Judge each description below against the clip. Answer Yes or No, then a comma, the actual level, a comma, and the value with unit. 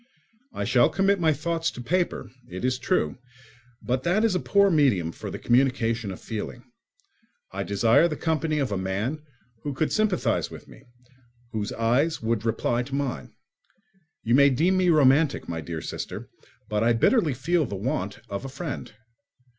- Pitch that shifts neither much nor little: No, wide, 6.3 semitones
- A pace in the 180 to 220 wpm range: No, average, 170 wpm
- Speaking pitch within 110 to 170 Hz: Yes, low, 135 Hz